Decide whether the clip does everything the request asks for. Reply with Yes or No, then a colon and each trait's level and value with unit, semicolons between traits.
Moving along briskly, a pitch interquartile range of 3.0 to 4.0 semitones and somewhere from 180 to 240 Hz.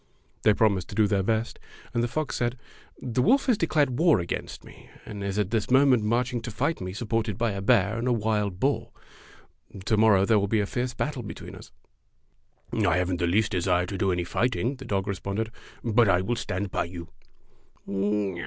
No: fast, 215 wpm; average, 3.7 semitones; low, 110 Hz